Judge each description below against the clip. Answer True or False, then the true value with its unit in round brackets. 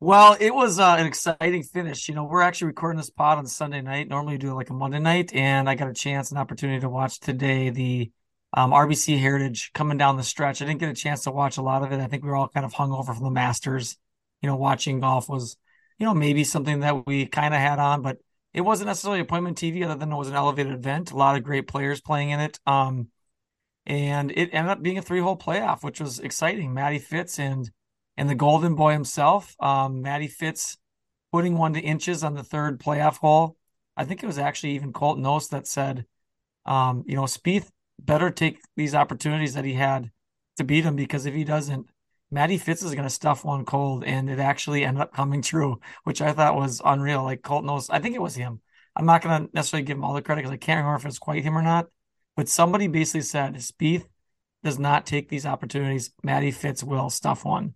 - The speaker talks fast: True (235 wpm)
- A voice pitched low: False (145 Hz)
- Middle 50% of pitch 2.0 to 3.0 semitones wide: True (2.6 semitones)